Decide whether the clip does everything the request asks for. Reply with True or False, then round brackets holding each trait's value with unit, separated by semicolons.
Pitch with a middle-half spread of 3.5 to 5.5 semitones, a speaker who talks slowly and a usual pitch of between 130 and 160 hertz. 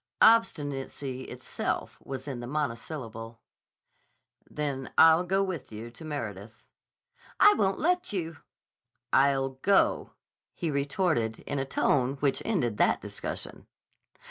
True (4.9 semitones; 115 wpm; 140 Hz)